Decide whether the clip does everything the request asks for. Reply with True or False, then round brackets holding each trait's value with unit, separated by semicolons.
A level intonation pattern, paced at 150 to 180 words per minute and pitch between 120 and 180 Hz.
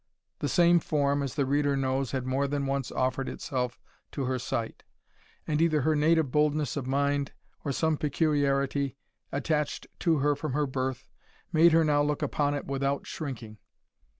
True (1.9 semitones; 170 wpm; 140 Hz)